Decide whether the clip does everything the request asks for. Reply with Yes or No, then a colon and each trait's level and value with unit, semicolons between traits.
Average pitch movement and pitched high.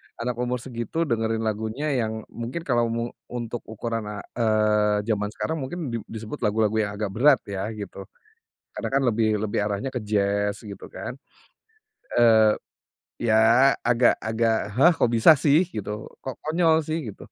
No: average, 3.0 semitones; low, 115 Hz